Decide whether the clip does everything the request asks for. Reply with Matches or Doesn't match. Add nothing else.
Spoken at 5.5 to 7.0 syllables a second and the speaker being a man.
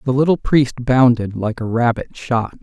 Doesn't match